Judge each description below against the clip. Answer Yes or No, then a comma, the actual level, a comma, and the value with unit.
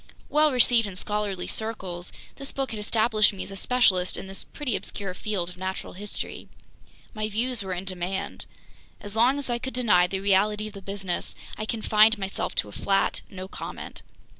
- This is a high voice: Yes, high, 205 Hz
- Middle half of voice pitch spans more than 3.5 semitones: No, average, 3.1 semitones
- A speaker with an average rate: Yes, average, 190 wpm